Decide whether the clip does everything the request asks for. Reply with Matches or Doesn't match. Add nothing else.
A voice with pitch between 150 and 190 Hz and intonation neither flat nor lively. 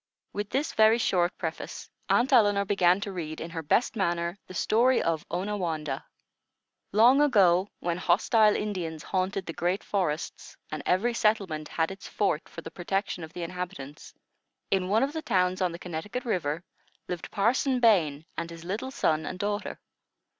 Matches